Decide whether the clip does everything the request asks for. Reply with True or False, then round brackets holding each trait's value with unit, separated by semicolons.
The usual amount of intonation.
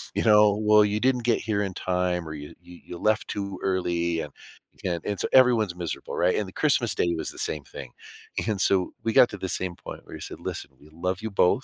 True (3.5 semitones)